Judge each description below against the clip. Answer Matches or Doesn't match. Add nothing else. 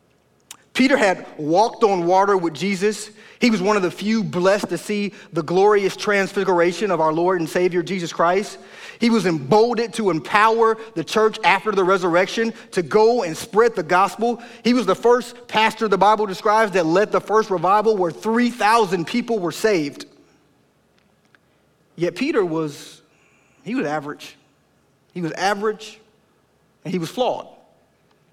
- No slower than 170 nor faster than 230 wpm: Doesn't match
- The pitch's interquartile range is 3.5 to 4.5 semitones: Matches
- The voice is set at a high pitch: Matches